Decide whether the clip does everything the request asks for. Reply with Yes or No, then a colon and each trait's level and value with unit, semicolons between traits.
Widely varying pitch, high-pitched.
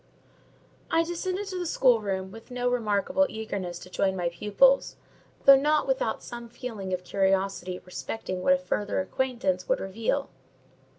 Yes: wide, 6.3 semitones; high, 225 Hz